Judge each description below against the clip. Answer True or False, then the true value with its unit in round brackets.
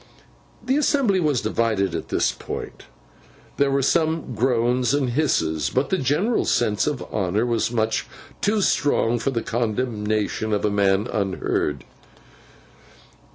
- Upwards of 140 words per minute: False (135 wpm)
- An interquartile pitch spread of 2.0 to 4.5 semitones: False (5.2 semitones)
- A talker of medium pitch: False (120 Hz)